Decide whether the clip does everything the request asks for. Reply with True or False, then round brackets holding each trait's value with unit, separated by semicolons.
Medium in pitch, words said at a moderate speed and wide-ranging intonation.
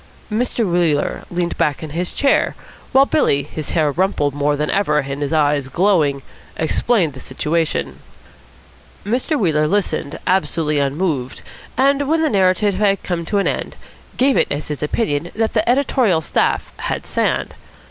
True (170 Hz; 155 wpm; 6.1 semitones)